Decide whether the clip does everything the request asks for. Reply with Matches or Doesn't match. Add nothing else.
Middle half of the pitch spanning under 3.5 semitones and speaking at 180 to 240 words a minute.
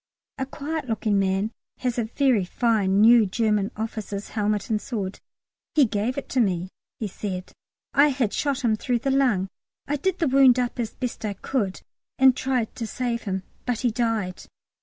Doesn't match